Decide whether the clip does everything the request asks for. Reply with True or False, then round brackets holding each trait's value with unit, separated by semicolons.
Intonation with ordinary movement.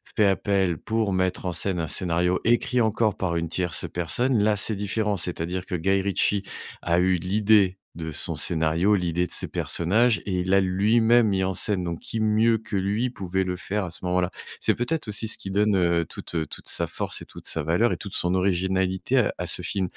True (3.1 semitones)